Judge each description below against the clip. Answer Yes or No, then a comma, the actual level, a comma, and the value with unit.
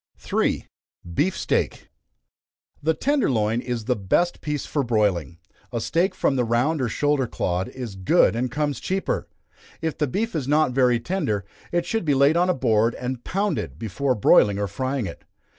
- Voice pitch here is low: Yes, low, 130 Hz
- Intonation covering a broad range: Yes, wide, 5.7 semitones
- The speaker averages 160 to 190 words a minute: Yes, average, 175 wpm